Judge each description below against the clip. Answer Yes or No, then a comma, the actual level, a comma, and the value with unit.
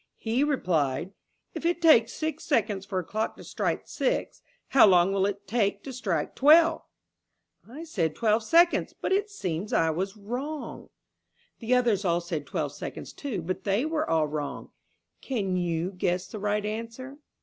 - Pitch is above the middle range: Yes, high, 210 Hz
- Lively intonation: Yes, wide, 6.9 semitones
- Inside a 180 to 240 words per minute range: No, average, 170 wpm